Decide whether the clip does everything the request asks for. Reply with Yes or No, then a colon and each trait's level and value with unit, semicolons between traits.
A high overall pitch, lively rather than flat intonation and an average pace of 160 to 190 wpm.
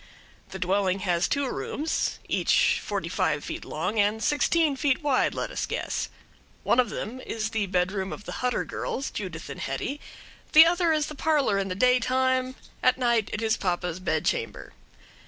Yes: high, 230 Hz; wide, 6.4 semitones; average, 175 wpm